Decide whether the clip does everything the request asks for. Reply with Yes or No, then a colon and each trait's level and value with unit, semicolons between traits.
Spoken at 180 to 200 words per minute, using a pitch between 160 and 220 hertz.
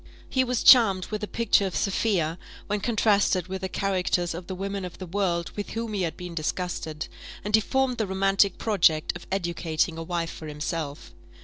Yes: average, 195 wpm; high, 190 Hz